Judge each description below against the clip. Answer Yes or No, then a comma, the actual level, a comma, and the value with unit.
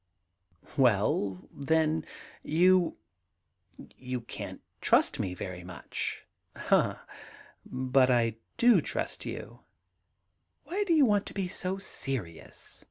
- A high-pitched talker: No, low, 135 Hz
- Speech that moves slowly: Yes, slow, 115 wpm